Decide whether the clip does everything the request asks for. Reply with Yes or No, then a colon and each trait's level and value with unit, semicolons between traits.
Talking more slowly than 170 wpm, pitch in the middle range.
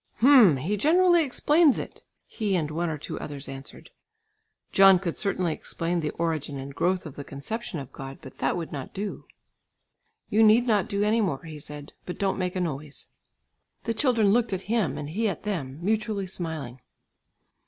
No: average, 185 wpm; medium, 180 Hz